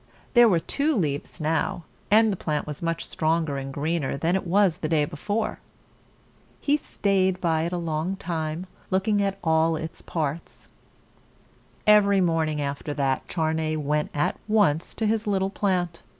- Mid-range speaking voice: Yes, medium, 165 Hz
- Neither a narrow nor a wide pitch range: Yes, average, 4.0 semitones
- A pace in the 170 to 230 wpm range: No, average, 160 wpm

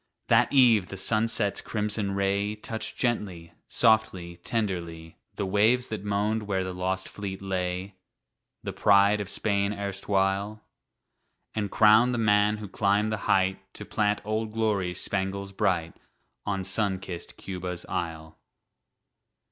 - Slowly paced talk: Yes, slow, 130 wpm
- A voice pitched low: Yes, low, 100 Hz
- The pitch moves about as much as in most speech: No, narrow, 2.2 semitones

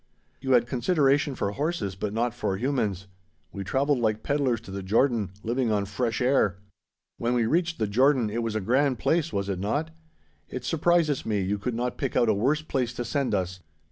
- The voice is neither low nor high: No, low, 120 Hz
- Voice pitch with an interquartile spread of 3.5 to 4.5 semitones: No, average, 5.1 semitones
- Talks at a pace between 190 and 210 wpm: Yes, fast, 205 wpm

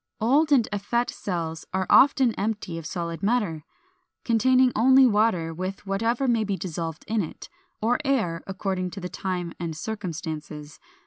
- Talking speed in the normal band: Yes, average, 150 wpm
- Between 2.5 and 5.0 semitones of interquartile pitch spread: No, wide, 5.6 semitones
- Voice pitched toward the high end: Yes, high, 195 Hz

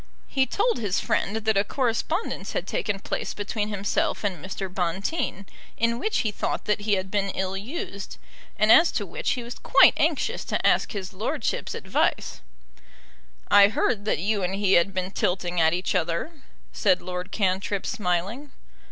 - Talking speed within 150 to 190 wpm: Yes, average, 170 wpm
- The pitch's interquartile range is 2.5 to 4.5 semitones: Yes, average, 3.2 semitones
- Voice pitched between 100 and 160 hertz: No, high, 200 Hz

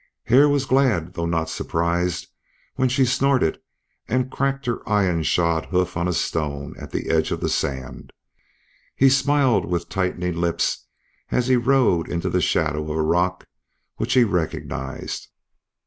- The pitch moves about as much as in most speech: No, wide, 7.6 semitones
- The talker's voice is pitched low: Yes, very low, 90 Hz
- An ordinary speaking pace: Yes, average, 155 wpm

